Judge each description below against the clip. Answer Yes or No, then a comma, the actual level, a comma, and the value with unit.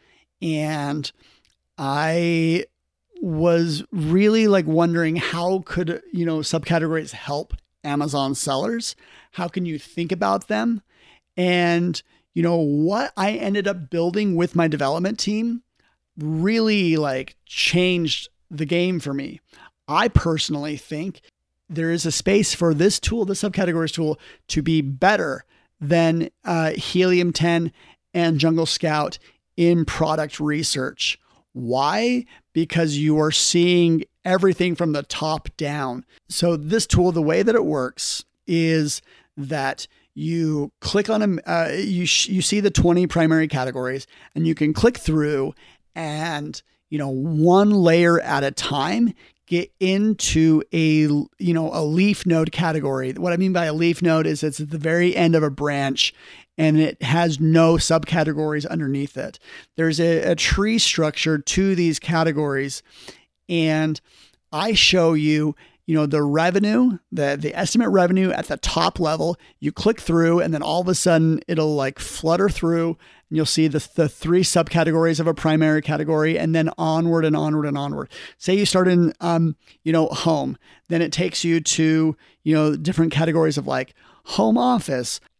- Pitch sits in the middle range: Yes, medium, 165 Hz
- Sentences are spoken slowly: No, average, 155 wpm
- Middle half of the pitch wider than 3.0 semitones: No, narrow, 2.4 semitones